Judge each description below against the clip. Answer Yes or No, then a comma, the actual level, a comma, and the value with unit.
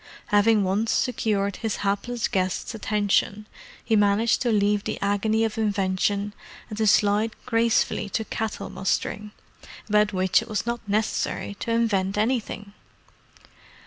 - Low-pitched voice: No, high, 210 Hz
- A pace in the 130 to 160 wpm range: Yes, slow, 135 wpm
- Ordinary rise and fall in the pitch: No, narrow, 1.8 semitones